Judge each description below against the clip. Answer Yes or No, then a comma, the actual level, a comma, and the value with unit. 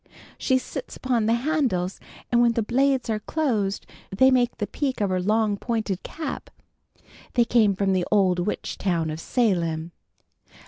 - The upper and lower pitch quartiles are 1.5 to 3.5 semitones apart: No, average, 4.7 semitones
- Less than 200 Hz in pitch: No, high, 215 Hz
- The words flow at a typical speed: Yes, average, 165 wpm